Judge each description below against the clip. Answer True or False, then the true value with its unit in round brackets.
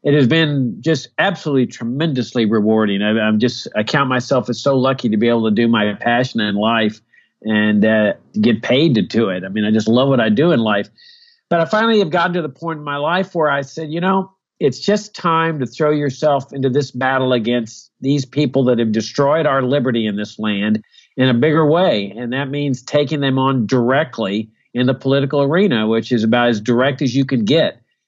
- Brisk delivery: True (220 wpm)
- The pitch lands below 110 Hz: False (130 Hz)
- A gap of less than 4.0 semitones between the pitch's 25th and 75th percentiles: False (4.6 semitones)